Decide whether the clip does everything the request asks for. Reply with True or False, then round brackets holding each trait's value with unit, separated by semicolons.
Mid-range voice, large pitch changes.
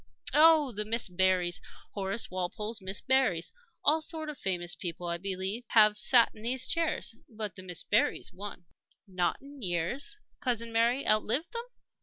False (215 Hz; 5.7 semitones)